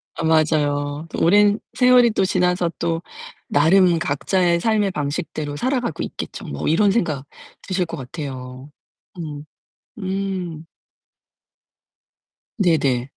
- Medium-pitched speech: Yes, medium, 165 Hz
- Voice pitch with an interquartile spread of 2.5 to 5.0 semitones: Yes, average, 4.7 semitones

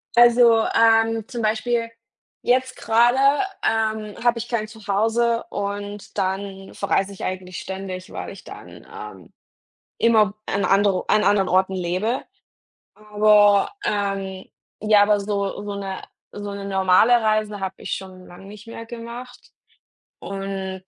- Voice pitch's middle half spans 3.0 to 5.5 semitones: No, narrow, 2.6 semitones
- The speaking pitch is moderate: No, high, 205 Hz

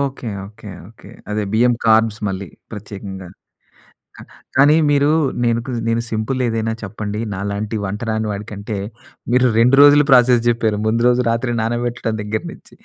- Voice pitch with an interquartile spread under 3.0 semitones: Yes, narrow, 2.6 semitones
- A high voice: No, low, 115 Hz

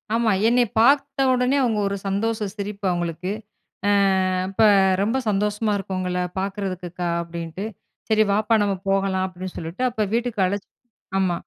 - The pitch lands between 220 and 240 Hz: No, high, 200 Hz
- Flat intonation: No, average, 3.3 semitones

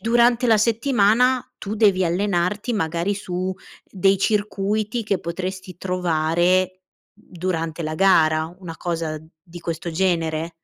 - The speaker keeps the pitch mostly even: No, average, 3.6 semitones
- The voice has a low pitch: No, medium, 185 Hz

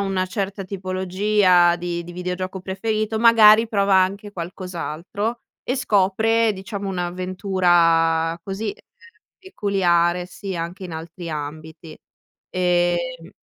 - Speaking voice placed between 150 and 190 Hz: Yes, medium, 185 Hz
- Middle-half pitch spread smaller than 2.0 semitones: No, narrow, 2.5 semitones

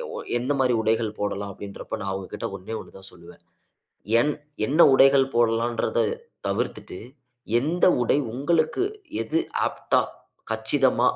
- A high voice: No, low, 115 Hz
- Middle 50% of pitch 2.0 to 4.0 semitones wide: No, average, 5.1 semitones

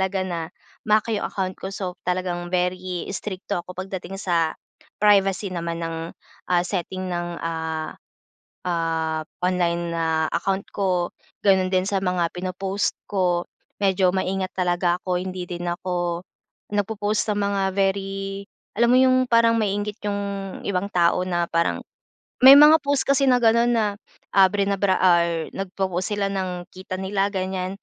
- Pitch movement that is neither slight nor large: No, narrow, 2.2 semitones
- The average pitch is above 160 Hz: Yes, medium, 185 Hz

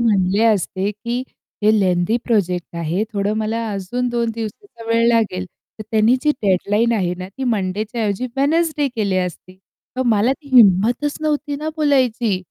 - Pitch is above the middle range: Yes, high, 220 Hz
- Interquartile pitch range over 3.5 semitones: Yes, average, 4.1 semitones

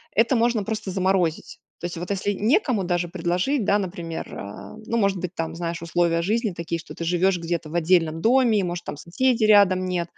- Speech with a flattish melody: No, average, 3.7 semitones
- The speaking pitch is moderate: Yes, medium, 180 Hz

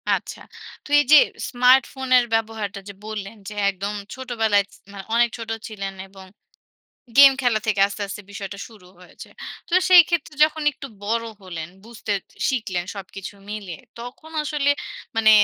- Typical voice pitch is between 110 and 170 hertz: No, high, 220 Hz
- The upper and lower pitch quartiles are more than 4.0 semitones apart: Yes, average, 4.4 semitones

